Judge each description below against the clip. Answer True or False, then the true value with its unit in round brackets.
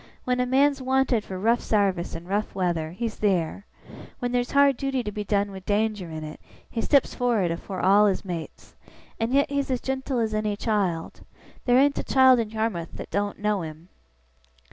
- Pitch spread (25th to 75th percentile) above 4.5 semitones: True (4.9 semitones)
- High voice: True (210 Hz)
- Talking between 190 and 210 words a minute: True (195 wpm)